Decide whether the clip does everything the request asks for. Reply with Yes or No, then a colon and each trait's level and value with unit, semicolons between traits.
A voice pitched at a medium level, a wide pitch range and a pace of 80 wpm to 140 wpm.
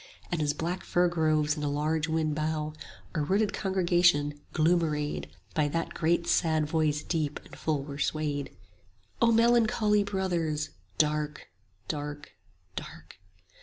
No: medium, 155 Hz; average, 2.7 semitones; slow, 135 wpm